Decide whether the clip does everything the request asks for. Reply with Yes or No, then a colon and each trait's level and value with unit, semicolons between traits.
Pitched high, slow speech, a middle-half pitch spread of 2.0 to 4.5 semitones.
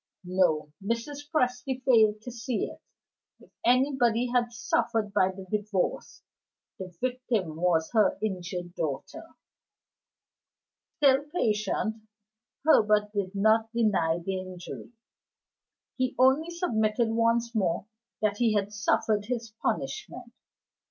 Yes: high, 220 Hz; slow, 110 wpm; average, 4.2 semitones